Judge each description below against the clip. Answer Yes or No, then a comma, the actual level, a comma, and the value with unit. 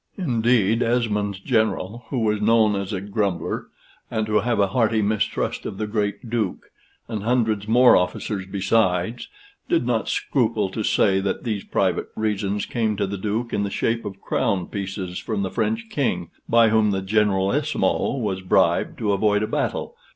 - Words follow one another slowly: No, average, 170 wpm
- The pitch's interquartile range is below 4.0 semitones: Yes, narrow, 2.6 semitones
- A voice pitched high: No, low, 105 Hz